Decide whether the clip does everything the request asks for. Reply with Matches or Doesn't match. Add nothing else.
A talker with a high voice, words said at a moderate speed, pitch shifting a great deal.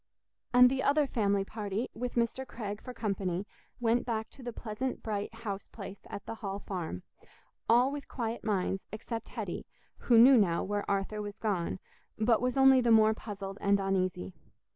Doesn't match